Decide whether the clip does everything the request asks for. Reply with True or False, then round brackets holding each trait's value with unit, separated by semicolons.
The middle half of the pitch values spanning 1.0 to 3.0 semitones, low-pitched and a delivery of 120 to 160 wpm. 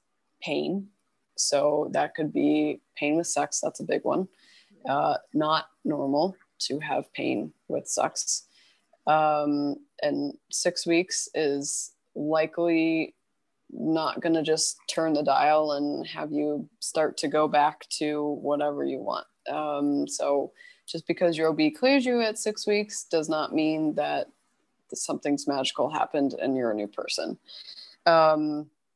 False (2.5 semitones; 155 Hz; 140 wpm)